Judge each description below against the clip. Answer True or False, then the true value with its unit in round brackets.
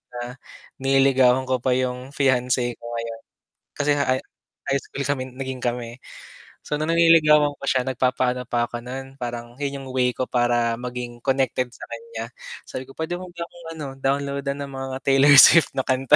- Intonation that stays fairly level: True (2.0 semitones)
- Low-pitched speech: True (130 Hz)